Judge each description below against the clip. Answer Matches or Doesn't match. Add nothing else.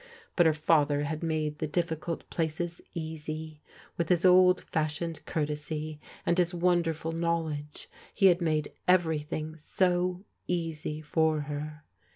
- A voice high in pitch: Doesn't match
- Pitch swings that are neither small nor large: Doesn't match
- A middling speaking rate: Doesn't match